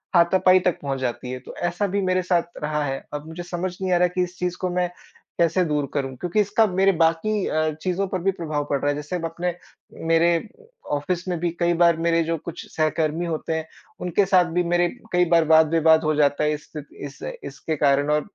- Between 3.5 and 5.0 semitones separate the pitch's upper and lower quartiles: No, average, 2.9 semitones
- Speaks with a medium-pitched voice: Yes, medium, 170 Hz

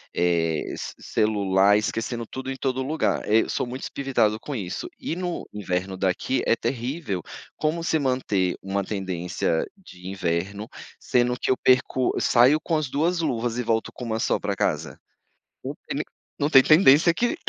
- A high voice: No, low, 120 Hz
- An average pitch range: No, wide, 5.7 semitones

